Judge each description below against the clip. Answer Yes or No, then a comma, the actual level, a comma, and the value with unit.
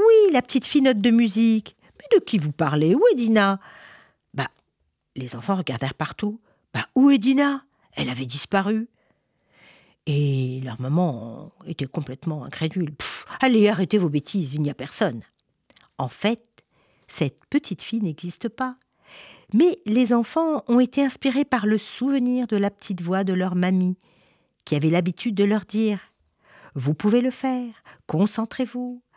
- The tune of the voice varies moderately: No, wide, 7.6 semitones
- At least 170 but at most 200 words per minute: No, average, 155 wpm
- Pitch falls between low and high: No, high, 205 Hz